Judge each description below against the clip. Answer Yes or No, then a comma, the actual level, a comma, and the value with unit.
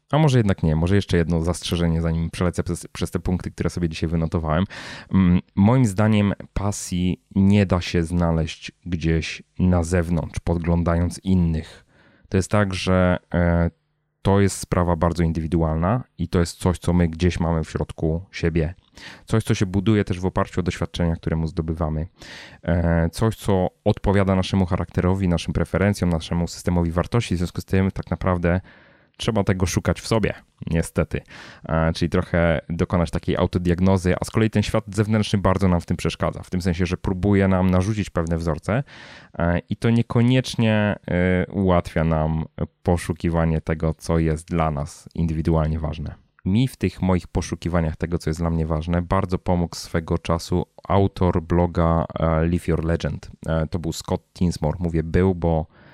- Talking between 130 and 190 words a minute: Yes, fast, 160 wpm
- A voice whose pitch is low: Yes, very low, 90 Hz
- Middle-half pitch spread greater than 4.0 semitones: No, narrow, 2.5 semitones